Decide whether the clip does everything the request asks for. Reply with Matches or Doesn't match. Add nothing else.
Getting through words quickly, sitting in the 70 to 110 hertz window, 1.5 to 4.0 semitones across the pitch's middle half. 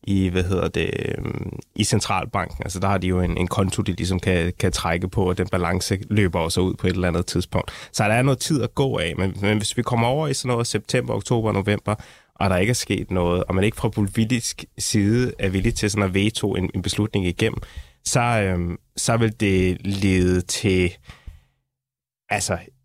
Doesn't match